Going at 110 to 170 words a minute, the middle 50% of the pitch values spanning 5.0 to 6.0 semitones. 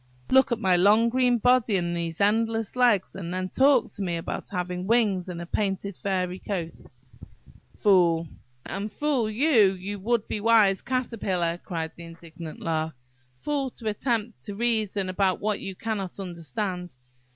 No: average, 160 wpm; average, 4.1 semitones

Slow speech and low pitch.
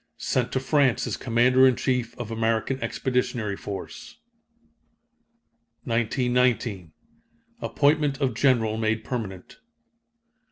Yes: slow, 95 wpm; low, 120 Hz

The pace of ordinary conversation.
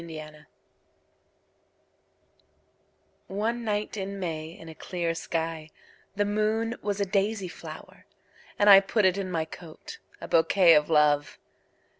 No: slow, 115 wpm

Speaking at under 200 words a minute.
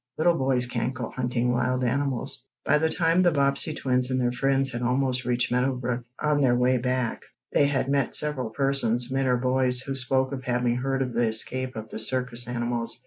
No: fast, 205 wpm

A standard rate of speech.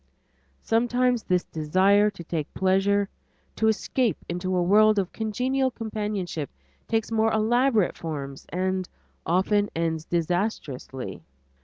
No: slow, 115 wpm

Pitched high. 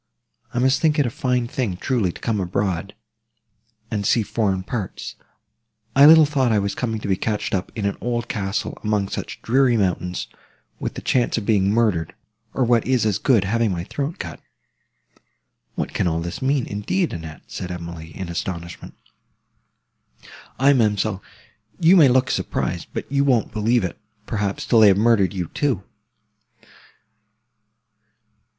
No: low, 110 Hz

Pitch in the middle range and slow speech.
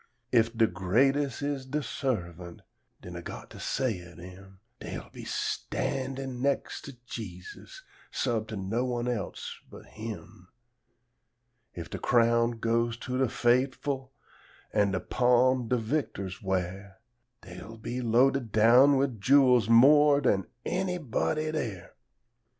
No: low, 120 Hz; slow, 130 wpm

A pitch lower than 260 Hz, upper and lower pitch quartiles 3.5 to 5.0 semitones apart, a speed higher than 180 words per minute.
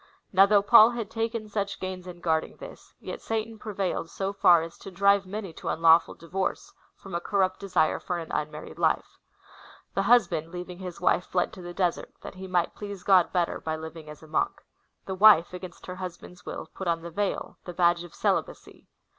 No: medium, 185 Hz; narrow, 2.6 semitones; fast, 205 wpm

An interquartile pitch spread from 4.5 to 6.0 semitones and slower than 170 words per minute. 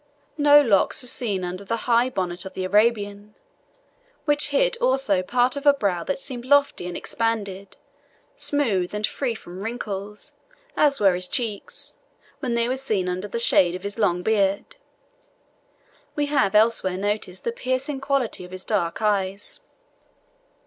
Yes: average, 5.2 semitones; average, 155 wpm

